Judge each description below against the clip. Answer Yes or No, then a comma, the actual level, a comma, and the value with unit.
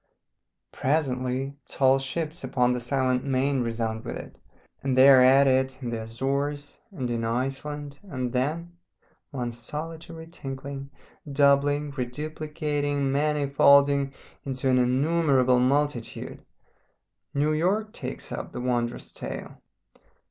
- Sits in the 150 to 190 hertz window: No, low, 135 Hz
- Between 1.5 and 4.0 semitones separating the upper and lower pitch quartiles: Yes, narrow, 2.5 semitones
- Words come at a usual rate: No, slow, 120 wpm